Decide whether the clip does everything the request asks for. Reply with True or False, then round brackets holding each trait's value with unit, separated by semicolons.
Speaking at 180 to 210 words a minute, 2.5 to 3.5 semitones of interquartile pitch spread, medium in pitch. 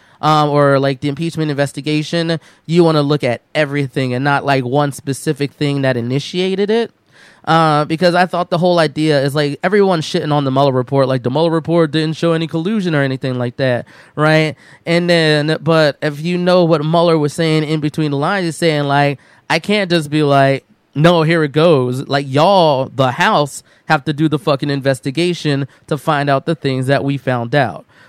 True (200 wpm; 2.9 semitones; 150 Hz)